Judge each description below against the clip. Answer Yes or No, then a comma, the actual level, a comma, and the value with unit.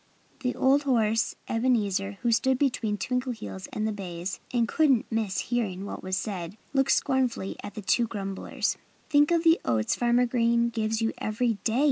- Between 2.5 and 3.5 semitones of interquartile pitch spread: No, average, 4.0 semitones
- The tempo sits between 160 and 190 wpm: Yes, average, 170 wpm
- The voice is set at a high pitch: Yes, high, 225 Hz